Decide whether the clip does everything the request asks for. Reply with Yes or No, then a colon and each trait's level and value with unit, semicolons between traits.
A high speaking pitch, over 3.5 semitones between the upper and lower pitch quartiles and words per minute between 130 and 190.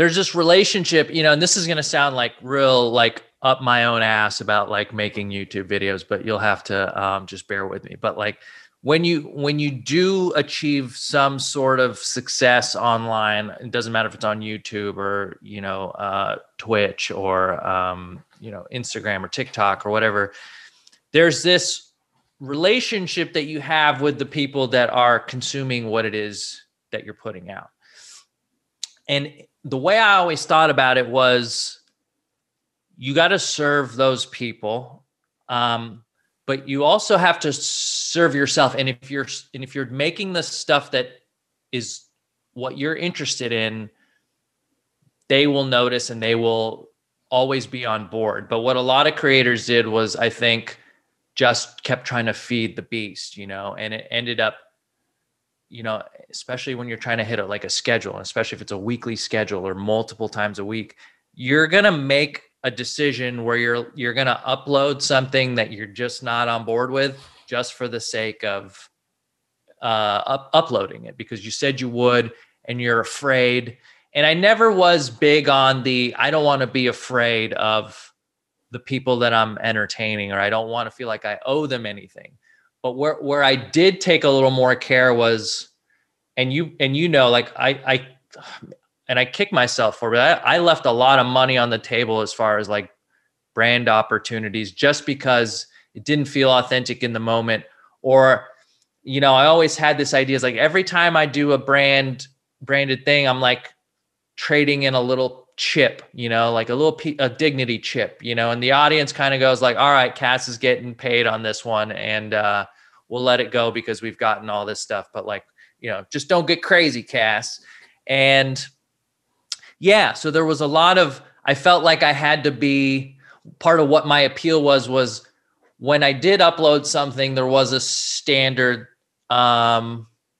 No: low, 130 Hz; average, 3.9 semitones; average, 185 wpm